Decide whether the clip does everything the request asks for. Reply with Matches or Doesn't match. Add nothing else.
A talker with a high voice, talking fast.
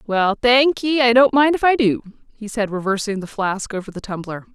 Matches